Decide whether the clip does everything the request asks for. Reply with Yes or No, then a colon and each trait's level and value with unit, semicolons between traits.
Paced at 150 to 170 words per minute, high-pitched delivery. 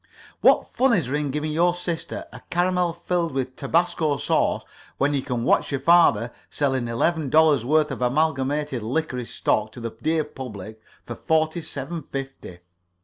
No: average, 165 wpm; medium, 145 Hz